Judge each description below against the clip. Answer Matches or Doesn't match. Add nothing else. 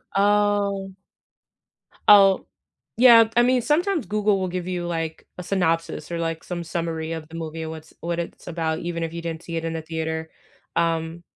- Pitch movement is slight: Doesn't match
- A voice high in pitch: Doesn't match